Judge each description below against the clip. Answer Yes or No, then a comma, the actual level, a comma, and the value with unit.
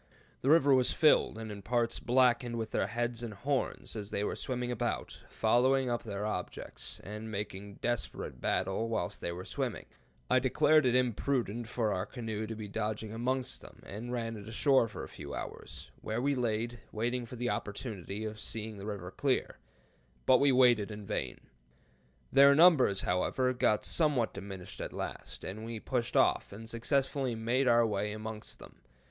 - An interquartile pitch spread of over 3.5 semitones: No, average, 3.0 semitones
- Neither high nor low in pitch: No, low, 115 Hz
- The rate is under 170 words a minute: No, average, 175 wpm